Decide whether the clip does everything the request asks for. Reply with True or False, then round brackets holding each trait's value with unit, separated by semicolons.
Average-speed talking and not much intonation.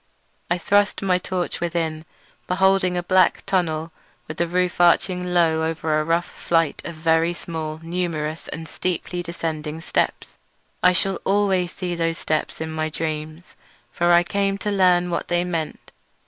True (160 wpm; 2.1 semitones)